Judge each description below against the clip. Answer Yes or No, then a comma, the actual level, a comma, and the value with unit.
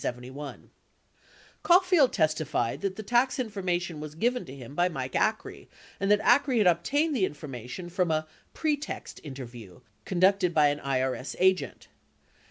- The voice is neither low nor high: Yes, medium, 175 Hz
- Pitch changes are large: Yes, wide, 7.6 semitones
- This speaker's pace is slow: No, average, 145 wpm